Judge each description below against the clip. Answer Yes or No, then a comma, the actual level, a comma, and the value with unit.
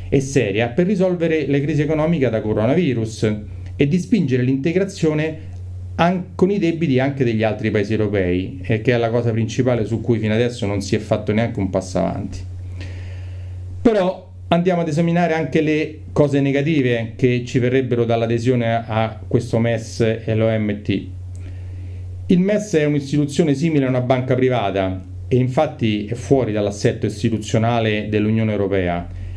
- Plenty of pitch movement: Yes, wide, 6.0 semitones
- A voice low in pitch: Yes, low, 115 Hz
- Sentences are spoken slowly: No, average, 150 wpm